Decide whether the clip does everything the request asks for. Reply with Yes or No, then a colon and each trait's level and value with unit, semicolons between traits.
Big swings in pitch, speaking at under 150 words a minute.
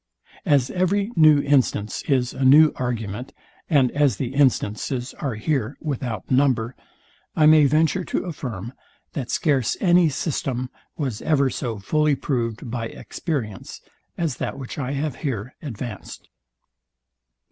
No: average, 3.9 semitones; slow, 135 wpm